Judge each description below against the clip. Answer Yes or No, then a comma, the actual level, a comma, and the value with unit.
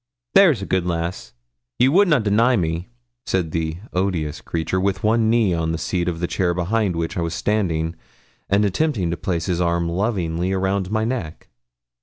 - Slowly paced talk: No, average, 185 wpm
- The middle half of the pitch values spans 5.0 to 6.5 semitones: No, average, 4.0 semitones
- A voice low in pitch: Yes, very low, 90 Hz